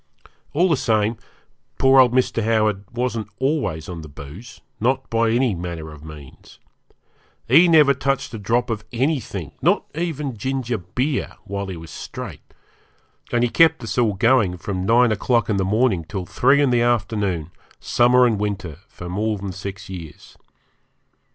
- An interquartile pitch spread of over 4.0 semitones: Yes, average, 5.1 semitones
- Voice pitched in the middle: No, low, 110 Hz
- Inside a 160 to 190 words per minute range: Yes, average, 165 wpm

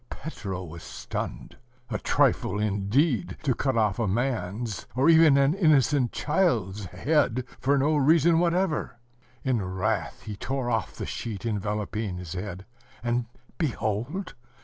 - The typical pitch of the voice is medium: No, low, 120 Hz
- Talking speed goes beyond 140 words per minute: No, slow, 135 wpm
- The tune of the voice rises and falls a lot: Yes, wide, 6.3 semitones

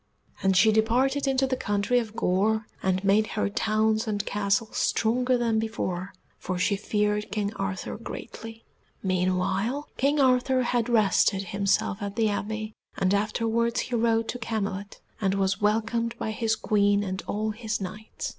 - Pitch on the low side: No, high, 215 Hz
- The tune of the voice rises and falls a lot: No, narrow, 2.4 semitones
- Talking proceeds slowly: No, average, 155 wpm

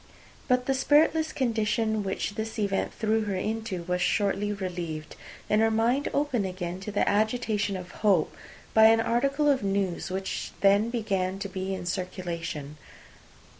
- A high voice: Yes, high, 205 Hz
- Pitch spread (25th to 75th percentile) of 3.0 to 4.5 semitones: Yes, average, 3.3 semitones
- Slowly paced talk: No, average, 155 wpm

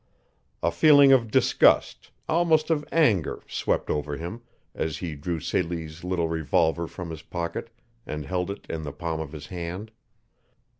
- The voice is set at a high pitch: No, very low, 85 Hz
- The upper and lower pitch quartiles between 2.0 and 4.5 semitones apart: No, average, 5.1 semitones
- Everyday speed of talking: Yes, average, 155 wpm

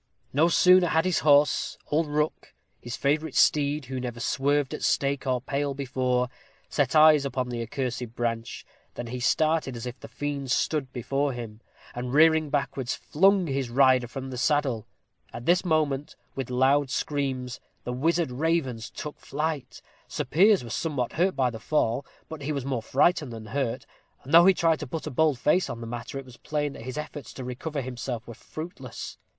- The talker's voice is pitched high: No, low, 135 Hz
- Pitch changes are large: No, average, 3.6 semitones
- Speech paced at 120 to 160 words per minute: No, average, 190 wpm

